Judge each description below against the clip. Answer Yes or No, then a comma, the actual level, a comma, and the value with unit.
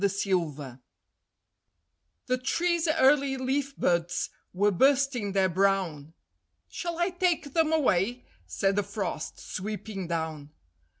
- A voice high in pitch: Yes, high, 205 Hz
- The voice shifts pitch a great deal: Yes, wide, 7.8 semitones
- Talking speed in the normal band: No, slow, 115 wpm